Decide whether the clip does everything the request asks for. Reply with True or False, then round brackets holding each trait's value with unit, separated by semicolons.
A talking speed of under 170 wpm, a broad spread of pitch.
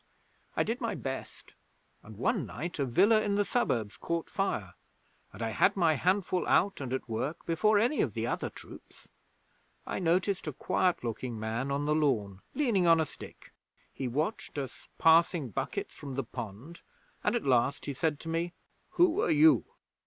False (180 wpm; 7.4 semitones)